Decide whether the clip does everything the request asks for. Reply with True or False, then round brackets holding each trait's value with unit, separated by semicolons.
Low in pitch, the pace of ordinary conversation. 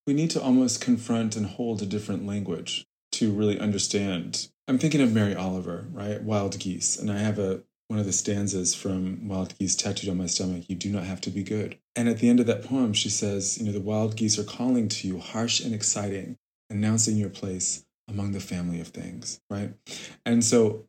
False (105 Hz; 215 wpm)